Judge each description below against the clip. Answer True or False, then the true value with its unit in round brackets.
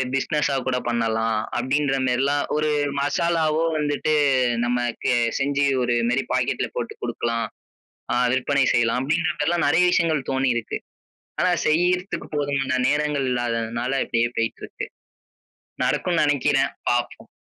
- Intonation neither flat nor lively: True (3.6 semitones)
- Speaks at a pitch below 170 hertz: True (135 Hz)